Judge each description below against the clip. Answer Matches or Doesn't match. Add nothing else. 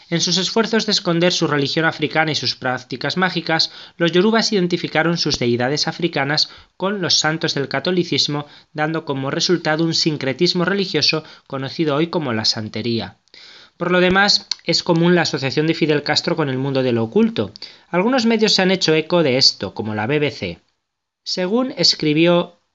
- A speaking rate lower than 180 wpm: Matches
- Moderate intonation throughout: Matches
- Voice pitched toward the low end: Doesn't match